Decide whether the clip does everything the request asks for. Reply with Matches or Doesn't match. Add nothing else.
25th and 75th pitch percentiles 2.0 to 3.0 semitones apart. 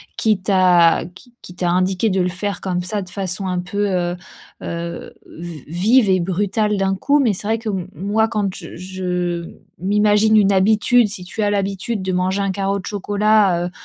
Matches